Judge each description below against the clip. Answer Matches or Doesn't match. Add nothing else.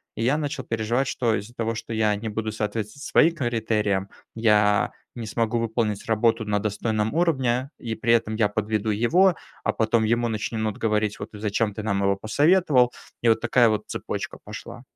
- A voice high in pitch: Doesn't match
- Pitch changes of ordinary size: Doesn't match